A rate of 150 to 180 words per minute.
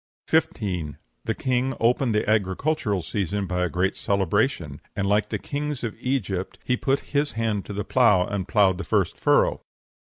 Yes: average, 175 wpm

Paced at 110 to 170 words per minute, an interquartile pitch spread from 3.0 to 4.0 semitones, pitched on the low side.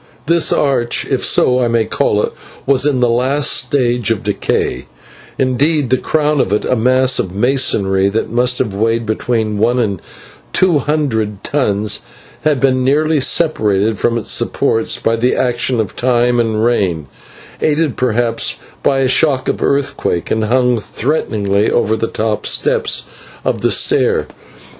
Yes: average, 145 wpm; average, 3.5 semitones; low, 120 Hz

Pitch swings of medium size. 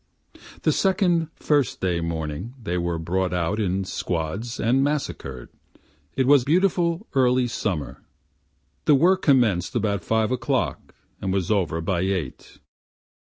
No: wide, 7.7 semitones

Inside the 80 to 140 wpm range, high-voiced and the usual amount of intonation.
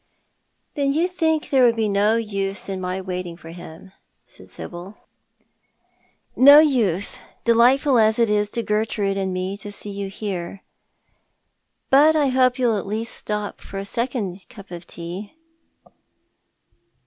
No: average, 155 wpm; high, 210 Hz; average, 4.4 semitones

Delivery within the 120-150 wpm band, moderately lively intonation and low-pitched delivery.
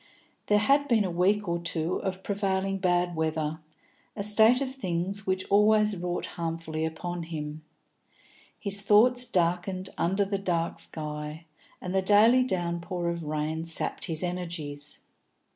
No: average, 145 wpm; average, 3.4 semitones; medium, 180 Hz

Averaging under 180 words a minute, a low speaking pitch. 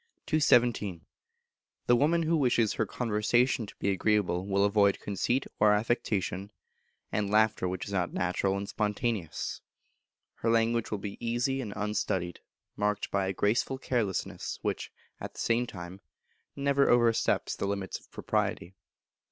Yes: average, 140 wpm; low, 105 Hz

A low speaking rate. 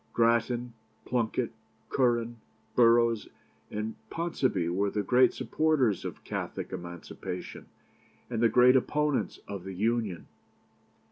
Yes: slow, 110 wpm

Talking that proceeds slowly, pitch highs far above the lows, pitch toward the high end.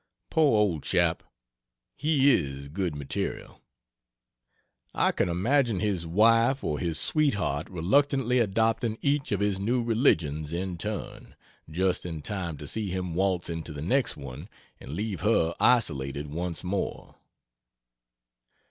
No: slow, 130 wpm; wide, 5.8 semitones; very low, 95 Hz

